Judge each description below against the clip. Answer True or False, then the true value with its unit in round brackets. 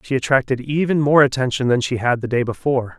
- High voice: False (130 Hz)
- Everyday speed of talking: False (220 wpm)